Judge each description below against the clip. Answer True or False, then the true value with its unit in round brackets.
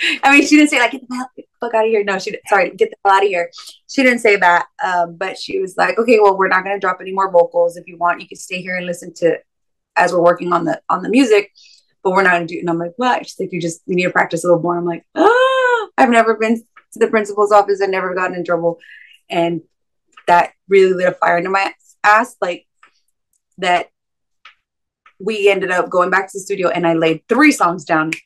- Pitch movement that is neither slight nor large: True (4.5 semitones)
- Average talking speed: False (255 wpm)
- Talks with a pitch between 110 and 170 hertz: False (190 Hz)